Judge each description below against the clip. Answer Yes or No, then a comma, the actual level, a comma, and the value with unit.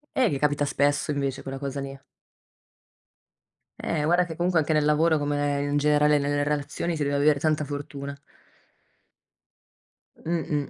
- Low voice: No, medium, 145 Hz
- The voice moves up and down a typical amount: No, narrow, 1.4 semitones